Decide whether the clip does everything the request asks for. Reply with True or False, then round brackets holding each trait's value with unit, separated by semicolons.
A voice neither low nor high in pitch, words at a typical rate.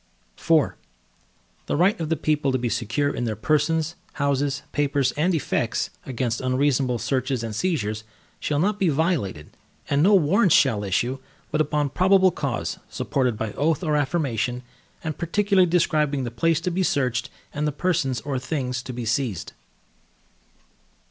True (145 Hz; 155 wpm)